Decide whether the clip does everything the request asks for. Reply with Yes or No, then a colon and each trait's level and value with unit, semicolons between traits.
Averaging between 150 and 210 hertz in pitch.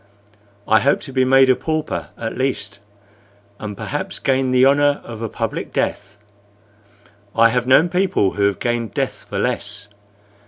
No: low, 125 Hz